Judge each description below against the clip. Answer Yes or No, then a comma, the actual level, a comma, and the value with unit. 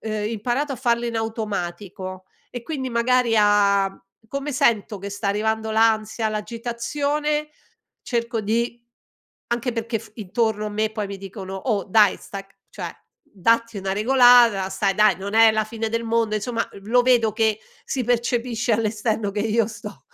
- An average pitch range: No, narrow, 2.3 semitones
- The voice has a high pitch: Yes, high, 220 Hz